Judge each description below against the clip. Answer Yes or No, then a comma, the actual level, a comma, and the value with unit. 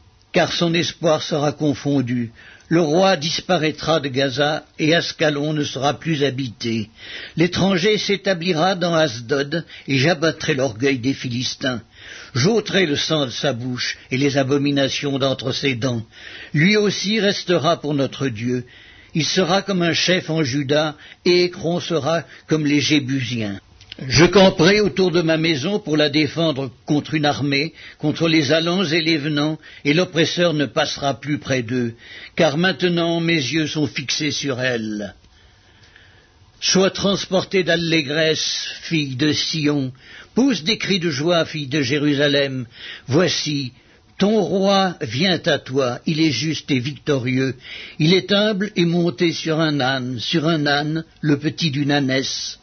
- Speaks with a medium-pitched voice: Yes, medium, 150 Hz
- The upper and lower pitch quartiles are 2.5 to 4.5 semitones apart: Yes, average, 3.9 semitones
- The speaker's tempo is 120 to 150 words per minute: Yes, slow, 145 wpm